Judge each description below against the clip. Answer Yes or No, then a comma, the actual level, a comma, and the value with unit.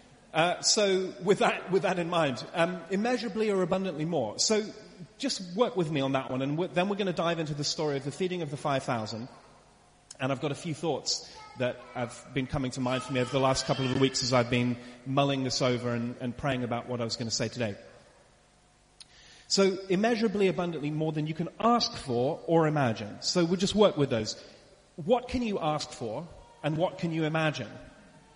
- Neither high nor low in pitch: Yes, medium, 155 Hz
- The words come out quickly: Yes, fast, 215 wpm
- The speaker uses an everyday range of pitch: No, wide, 6.5 semitones